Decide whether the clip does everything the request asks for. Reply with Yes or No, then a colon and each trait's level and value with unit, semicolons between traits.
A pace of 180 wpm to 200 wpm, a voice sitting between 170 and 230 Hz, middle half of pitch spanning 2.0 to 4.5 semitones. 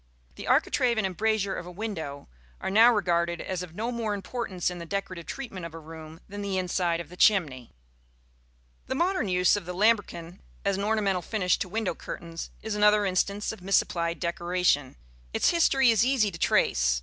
Yes: average, 185 wpm; high, 190 Hz; average, 3.9 semitones